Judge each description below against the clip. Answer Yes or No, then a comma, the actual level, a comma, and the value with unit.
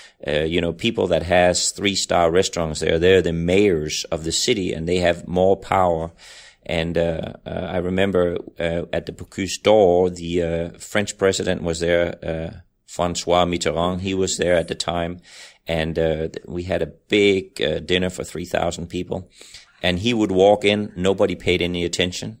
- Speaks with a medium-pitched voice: No, very low, 90 Hz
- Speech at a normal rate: Yes, average, 175 wpm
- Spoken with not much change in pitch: Yes, narrow, 1.9 semitones